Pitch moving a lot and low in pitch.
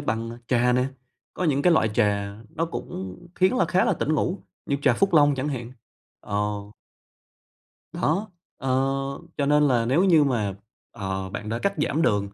Yes: wide, 6.9 semitones; low, 130 Hz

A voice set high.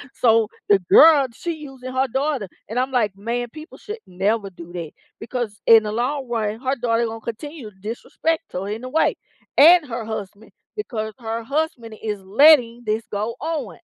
Yes: high, 230 Hz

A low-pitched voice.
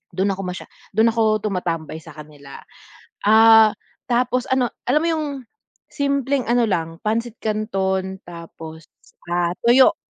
No: high, 215 Hz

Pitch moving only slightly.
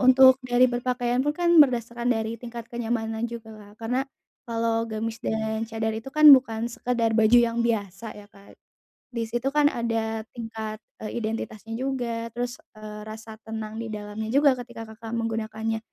Yes: narrow, 1.7 semitones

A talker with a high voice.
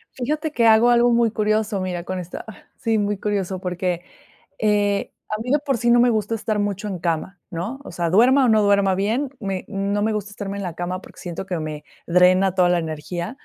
Yes: high, 200 Hz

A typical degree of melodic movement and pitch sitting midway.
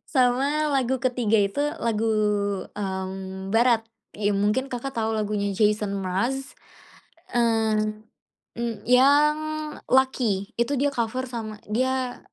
No: average, 3.7 semitones; high, 225 Hz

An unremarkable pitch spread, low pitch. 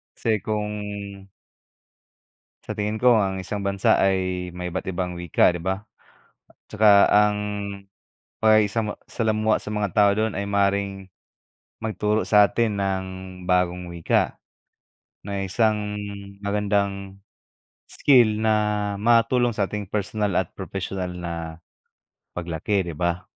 No: narrow, 2.2 semitones; low, 100 Hz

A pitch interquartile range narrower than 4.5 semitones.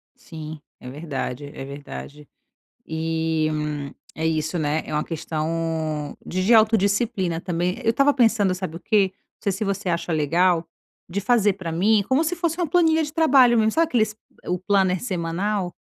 No: average, 5.3 semitones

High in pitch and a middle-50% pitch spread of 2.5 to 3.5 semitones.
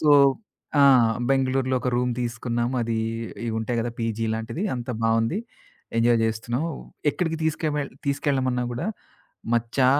No: low, 125 Hz; average, 2.9 semitones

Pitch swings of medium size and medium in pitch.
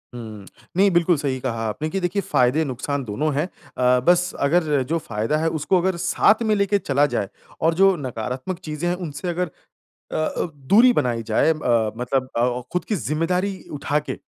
No: wide, 6.0 semitones; medium, 150 Hz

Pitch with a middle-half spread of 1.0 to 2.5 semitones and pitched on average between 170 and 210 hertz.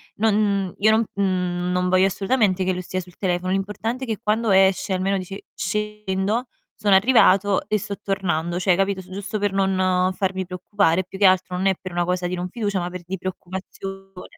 Yes: narrow, 1.8 semitones; high, 190 Hz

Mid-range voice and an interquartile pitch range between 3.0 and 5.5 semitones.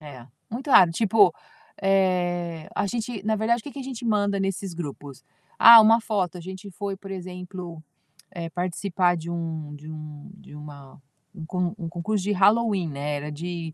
Yes: medium, 180 Hz; average, 3.8 semitones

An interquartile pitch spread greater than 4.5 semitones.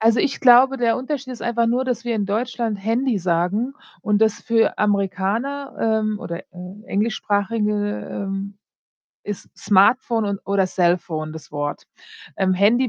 No: average, 3.6 semitones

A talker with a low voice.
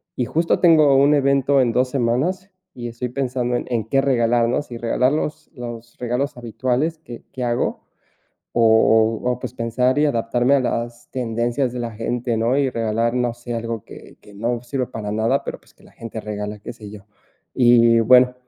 Yes: low, 120 Hz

